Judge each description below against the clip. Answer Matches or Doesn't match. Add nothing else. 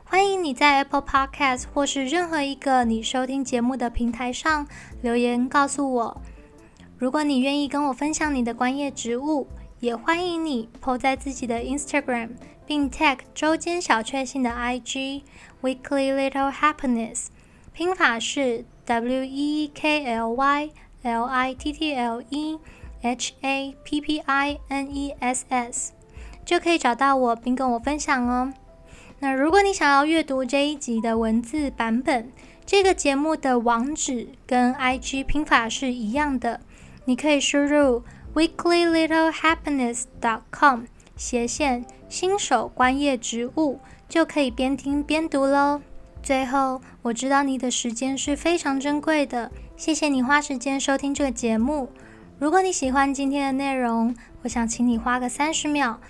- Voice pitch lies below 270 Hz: Doesn't match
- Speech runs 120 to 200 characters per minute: Doesn't match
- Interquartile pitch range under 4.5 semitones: Matches